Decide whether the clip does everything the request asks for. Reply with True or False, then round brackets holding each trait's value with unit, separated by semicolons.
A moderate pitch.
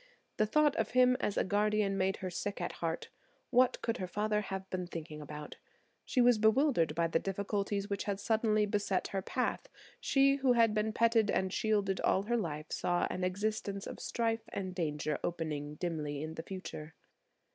False (200 Hz)